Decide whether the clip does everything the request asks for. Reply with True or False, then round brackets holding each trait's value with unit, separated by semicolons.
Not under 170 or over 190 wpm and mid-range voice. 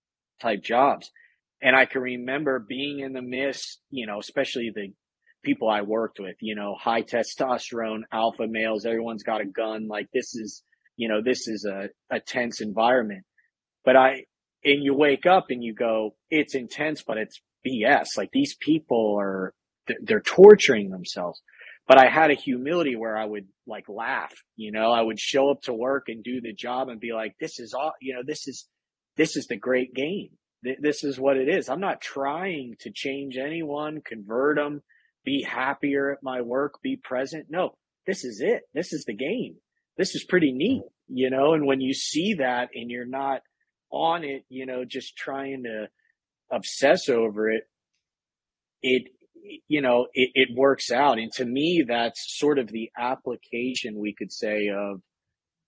False (180 wpm; 130 Hz)